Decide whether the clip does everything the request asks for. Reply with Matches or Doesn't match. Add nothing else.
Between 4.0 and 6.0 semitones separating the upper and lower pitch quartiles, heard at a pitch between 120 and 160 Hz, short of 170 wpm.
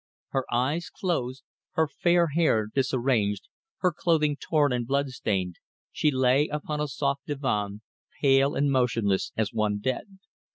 Matches